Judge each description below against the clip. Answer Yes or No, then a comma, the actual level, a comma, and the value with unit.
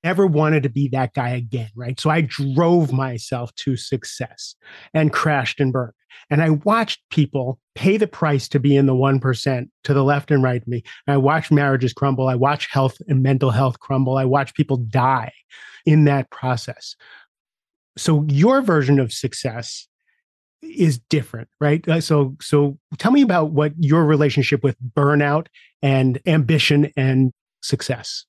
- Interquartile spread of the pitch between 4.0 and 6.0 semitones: No, average, 2.7 semitones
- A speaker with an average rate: Yes, average, 170 wpm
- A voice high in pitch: No, medium, 140 Hz